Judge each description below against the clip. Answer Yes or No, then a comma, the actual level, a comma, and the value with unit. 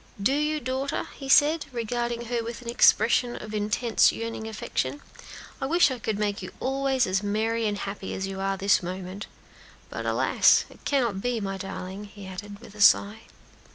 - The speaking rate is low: No, average, 190 wpm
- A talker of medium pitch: No, high, 220 Hz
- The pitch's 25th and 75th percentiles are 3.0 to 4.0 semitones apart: Yes, average, 3.7 semitones